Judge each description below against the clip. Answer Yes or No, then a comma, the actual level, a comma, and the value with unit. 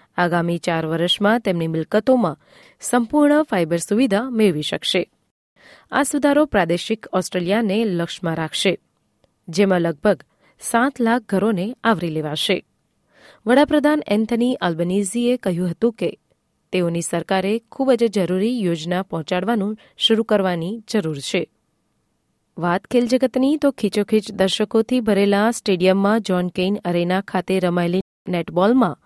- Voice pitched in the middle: No, high, 200 Hz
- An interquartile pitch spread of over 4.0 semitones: Yes, average, 4.7 semitones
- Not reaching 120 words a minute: Yes, average, 110 wpm